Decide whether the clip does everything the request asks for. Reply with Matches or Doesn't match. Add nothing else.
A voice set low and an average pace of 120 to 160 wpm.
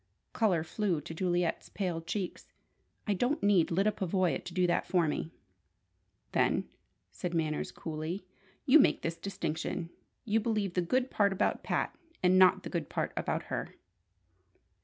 Doesn't match